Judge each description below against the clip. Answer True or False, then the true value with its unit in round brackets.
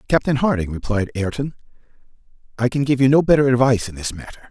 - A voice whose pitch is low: True (125 Hz)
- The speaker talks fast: False (185 wpm)